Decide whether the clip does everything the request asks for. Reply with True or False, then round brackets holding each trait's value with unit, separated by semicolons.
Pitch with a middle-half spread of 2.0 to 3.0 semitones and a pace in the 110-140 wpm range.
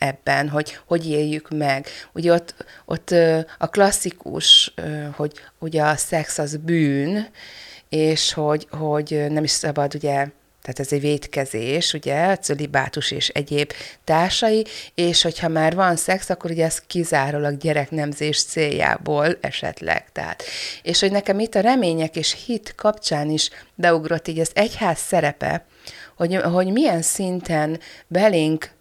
True (2.6 semitones; 135 wpm)